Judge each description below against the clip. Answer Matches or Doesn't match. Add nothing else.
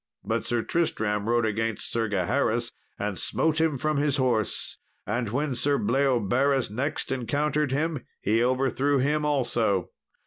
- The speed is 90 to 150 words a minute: Matches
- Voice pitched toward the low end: Matches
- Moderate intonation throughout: Matches